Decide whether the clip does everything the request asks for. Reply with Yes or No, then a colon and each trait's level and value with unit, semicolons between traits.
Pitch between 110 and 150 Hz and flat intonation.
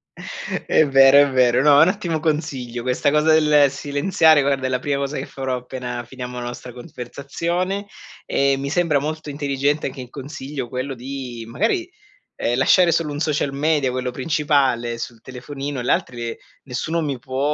No: medium, 140 Hz; average, 3.1 semitones